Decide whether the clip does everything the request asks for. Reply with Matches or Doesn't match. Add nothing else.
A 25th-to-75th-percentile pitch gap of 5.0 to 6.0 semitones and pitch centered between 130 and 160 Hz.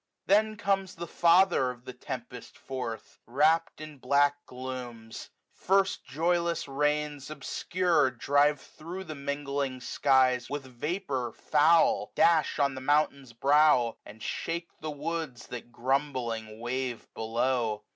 Doesn't match